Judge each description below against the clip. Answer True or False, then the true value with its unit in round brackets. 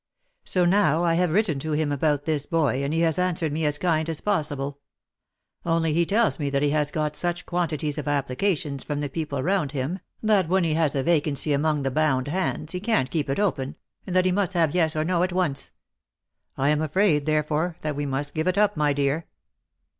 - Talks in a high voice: False (155 Hz)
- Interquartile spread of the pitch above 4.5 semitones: False (3.3 semitones)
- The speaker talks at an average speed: False (220 wpm)